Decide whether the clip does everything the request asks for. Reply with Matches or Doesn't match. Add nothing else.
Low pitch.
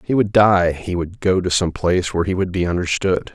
Matches